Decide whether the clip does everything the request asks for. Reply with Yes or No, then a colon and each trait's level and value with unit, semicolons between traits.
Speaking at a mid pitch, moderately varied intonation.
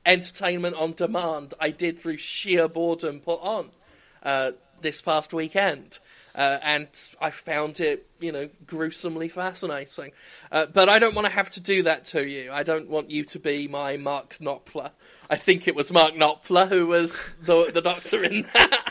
Yes: medium, 165 Hz; average, 3.1 semitones